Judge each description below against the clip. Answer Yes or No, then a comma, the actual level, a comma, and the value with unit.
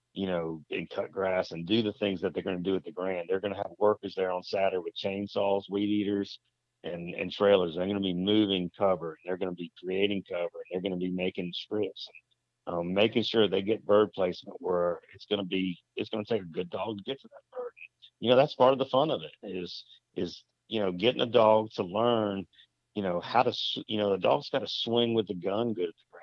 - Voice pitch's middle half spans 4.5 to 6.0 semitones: No, narrow, 2.6 semitones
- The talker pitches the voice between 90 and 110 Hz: Yes, low, 100 Hz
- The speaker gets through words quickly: Yes, fast, 250 wpm